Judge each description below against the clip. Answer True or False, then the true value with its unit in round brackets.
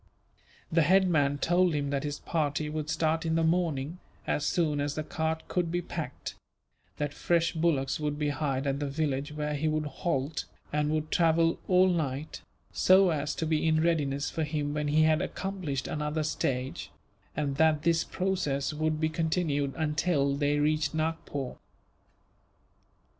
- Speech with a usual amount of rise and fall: False (2.1 semitones)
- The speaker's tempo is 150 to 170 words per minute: True (165 wpm)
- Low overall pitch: False (155 Hz)